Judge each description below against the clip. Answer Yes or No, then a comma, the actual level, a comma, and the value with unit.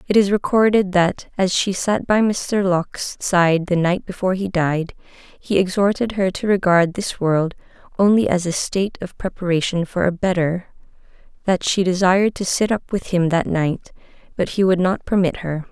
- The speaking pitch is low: No, medium, 185 Hz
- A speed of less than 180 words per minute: No, average, 185 wpm